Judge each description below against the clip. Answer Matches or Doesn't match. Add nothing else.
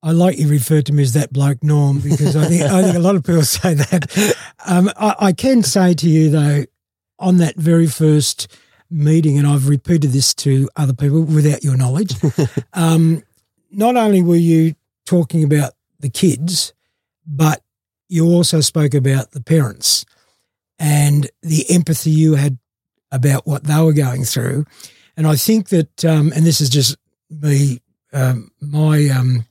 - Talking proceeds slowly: Doesn't match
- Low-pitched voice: Doesn't match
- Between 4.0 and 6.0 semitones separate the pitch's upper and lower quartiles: Doesn't match